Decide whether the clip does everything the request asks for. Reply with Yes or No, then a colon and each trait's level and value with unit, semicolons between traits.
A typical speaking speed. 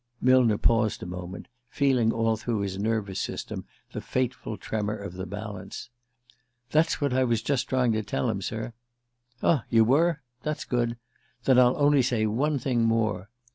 Yes: average, 175 wpm